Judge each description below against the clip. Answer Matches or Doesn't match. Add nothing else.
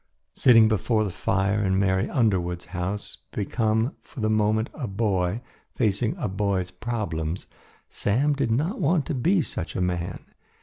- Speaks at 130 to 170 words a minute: Matches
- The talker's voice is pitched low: Matches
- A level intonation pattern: Doesn't match